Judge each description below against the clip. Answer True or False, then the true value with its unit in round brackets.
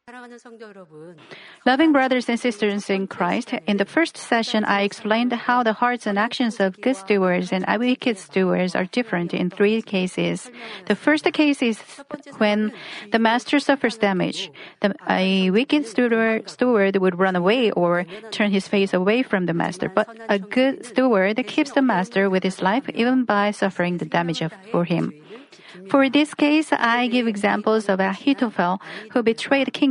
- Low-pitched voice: False (215 Hz)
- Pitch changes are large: False (4.2 semitones)